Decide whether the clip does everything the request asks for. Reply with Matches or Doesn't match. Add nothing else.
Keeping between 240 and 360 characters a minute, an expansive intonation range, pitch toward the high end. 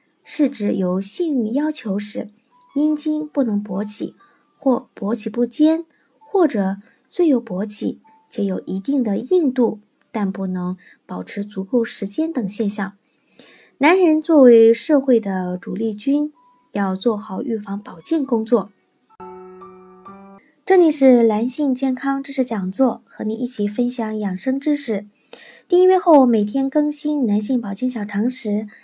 Doesn't match